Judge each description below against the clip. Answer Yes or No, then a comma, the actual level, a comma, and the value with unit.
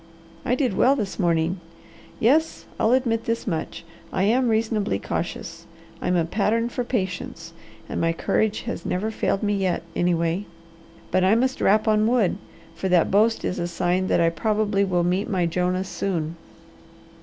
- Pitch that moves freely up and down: No, average, 4.0 semitones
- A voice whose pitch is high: Yes, high, 195 Hz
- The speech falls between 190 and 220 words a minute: No, average, 165 wpm